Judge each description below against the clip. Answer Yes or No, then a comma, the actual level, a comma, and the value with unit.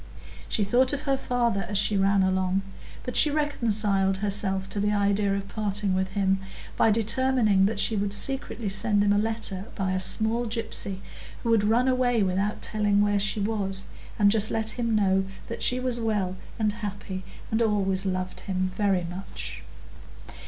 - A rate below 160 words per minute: No, average, 175 wpm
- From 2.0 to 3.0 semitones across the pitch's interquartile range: Yes, narrow, 2.6 semitones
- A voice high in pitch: Yes, high, 205 Hz